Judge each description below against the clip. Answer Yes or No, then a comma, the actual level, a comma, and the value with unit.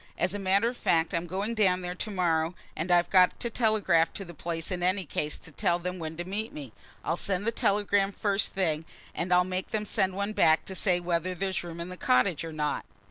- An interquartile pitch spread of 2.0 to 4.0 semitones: Yes, average, 2.8 semitones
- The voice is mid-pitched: Yes, medium, 180 Hz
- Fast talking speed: Yes, fast, 240 wpm